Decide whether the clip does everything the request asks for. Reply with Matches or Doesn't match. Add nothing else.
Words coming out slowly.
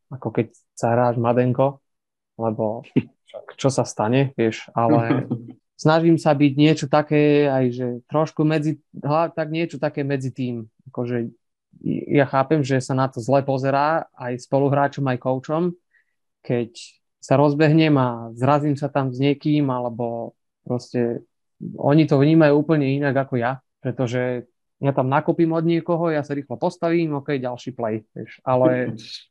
Doesn't match